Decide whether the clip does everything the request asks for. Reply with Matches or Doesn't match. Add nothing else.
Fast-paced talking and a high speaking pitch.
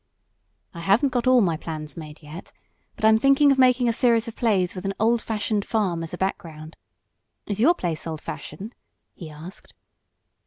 Doesn't match